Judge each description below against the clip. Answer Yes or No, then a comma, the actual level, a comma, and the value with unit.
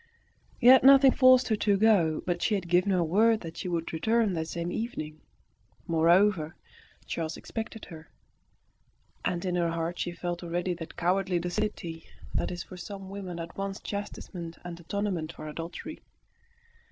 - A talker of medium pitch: Yes, medium, 175 Hz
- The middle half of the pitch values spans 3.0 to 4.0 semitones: Yes, average, 3.5 semitones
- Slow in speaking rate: No, average, 165 wpm